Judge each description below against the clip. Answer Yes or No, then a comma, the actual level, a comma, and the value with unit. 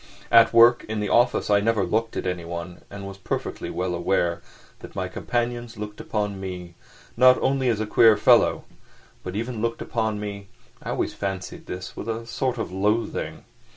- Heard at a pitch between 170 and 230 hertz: No, low, 105 Hz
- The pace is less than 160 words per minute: No, average, 170 wpm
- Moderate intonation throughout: Yes, average, 3.3 semitones